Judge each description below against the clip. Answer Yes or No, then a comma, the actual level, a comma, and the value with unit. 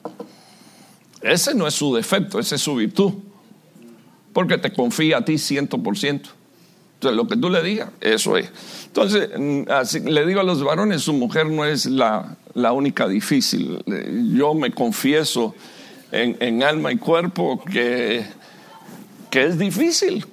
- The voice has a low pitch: No, medium, 160 Hz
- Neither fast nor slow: Yes, average, 150 wpm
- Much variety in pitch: Yes, wide, 6.8 semitones